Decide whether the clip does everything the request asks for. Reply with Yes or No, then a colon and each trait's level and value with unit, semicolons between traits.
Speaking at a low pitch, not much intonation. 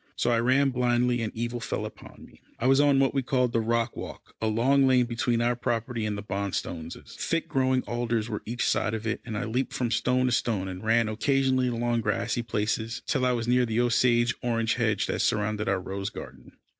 Yes: low, 120 Hz; narrow, 2.2 semitones